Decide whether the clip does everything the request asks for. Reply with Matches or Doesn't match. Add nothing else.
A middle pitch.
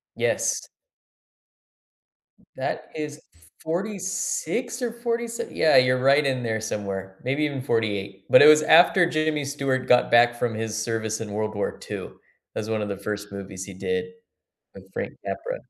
Doesn't match